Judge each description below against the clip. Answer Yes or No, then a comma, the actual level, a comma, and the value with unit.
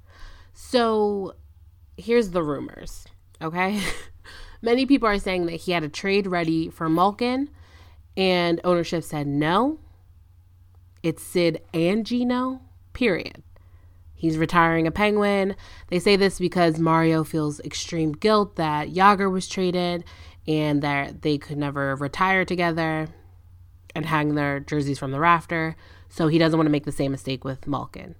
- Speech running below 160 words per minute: Yes, average, 145 wpm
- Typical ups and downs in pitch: No, wide, 7.0 semitones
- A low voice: No, medium, 160 Hz